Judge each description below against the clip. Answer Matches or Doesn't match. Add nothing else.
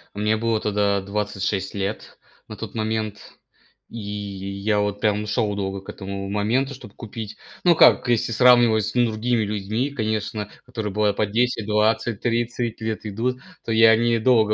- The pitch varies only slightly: Matches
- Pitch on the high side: Doesn't match